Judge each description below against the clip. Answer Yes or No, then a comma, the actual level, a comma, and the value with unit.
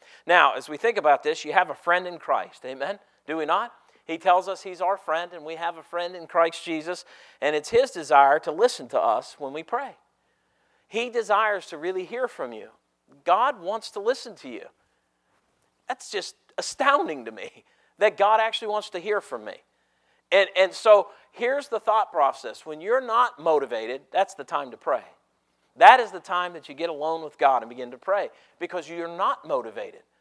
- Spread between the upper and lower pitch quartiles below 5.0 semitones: No, wide, 5.5 semitones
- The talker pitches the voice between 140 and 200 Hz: Yes, medium, 185 Hz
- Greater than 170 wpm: Yes, average, 200 wpm